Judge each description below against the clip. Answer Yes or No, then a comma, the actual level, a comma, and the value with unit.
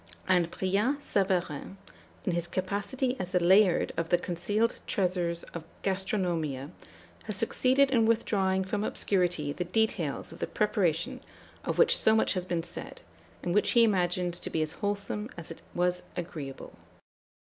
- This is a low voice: No, medium, 185 Hz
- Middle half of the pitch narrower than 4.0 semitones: Yes, average, 3.4 semitones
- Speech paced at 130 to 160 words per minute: Yes, average, 155 wpm